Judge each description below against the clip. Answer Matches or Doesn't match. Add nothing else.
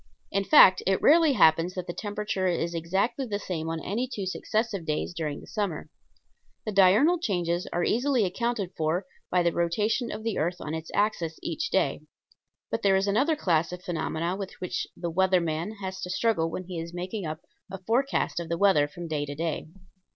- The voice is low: Doesn't match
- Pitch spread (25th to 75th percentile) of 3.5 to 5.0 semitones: Matches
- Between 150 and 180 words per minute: Doesn't match